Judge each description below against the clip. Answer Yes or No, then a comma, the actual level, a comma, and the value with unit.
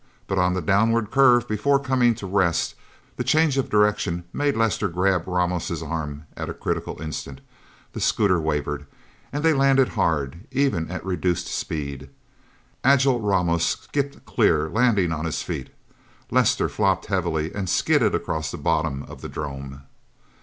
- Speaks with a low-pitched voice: Yes, very low, 95 Hz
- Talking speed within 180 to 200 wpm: No, average, 155 wpm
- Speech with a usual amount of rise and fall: No, wide, 7.2 semitones